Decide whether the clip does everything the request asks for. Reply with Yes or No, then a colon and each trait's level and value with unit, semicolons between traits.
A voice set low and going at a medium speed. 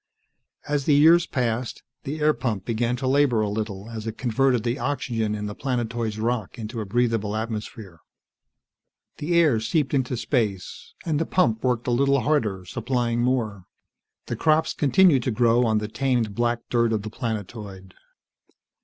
Yes: low, 120 Hz; average, 165 wpm